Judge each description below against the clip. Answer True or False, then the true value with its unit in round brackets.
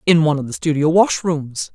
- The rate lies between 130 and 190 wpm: False (205 wpm)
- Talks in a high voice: False (155 Hz)